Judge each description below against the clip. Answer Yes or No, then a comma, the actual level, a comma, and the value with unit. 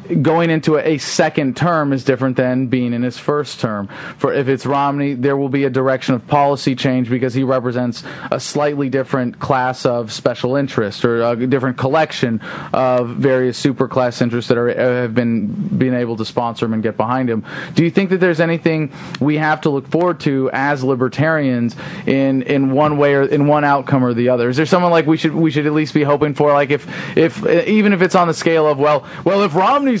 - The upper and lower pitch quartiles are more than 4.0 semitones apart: No, average, 3.5 semitones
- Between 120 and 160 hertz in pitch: Yes, medium, 140 Hz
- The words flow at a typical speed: No, fast, 220 wpm